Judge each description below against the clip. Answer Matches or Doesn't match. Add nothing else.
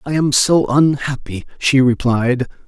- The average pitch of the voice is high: Doesn't match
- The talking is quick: Doesn't match